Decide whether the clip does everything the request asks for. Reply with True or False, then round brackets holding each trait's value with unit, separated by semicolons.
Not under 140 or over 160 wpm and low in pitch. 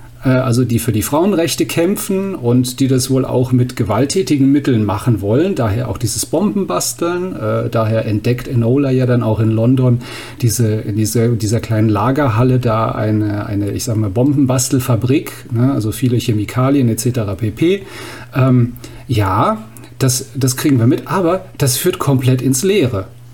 True (145 wpm; 125 Hz)